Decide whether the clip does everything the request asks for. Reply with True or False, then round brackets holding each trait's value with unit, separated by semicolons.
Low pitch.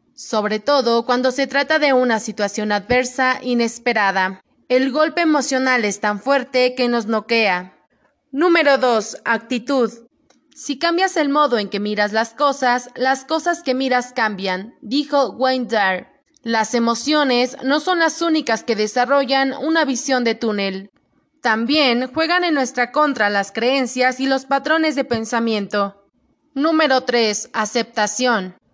False (250 Hz)